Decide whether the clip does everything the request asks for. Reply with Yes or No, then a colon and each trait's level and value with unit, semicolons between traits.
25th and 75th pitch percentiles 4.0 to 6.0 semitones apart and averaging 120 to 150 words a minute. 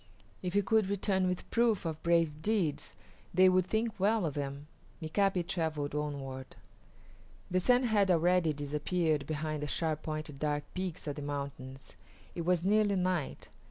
No: average, 4.3 semitones; average, 160 wpm